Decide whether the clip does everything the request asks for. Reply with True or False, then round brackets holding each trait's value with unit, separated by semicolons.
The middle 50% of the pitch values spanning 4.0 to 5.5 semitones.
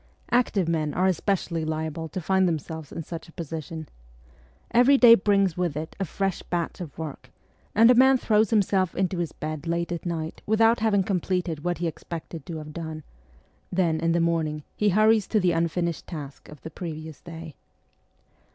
False (3.3 semitones)